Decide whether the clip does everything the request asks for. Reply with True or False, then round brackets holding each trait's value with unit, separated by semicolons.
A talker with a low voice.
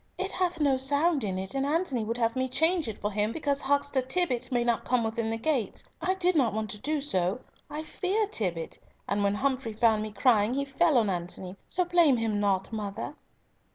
False (250 Hz)